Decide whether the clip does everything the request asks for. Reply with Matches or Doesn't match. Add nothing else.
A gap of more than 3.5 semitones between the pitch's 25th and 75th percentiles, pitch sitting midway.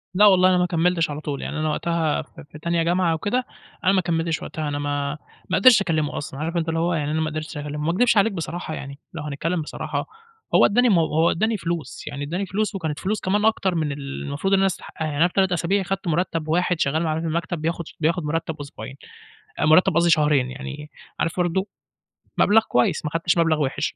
Doesn't match